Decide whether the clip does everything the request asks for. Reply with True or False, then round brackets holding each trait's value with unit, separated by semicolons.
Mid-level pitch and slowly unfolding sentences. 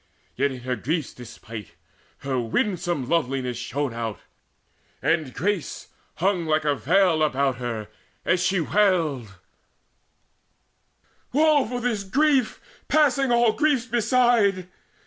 True (170 Hz; 115 wpm)